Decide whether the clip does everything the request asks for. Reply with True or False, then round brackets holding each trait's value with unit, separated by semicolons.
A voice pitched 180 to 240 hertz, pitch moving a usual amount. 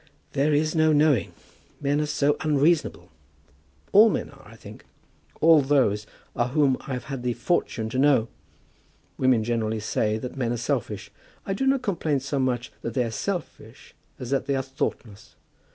False (135 Hz; 4.1 semitones)